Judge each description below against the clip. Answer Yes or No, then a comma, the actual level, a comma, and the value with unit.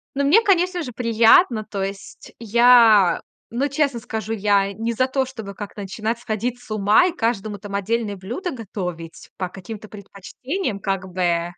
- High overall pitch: Yes, high, 220 Hz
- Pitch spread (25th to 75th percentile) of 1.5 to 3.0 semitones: No, average, 3.8 semitones